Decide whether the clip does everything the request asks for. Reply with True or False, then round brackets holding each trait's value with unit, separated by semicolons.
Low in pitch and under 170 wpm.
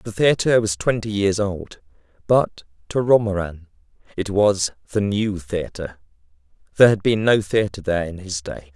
True (100 Hz; 160 wpm)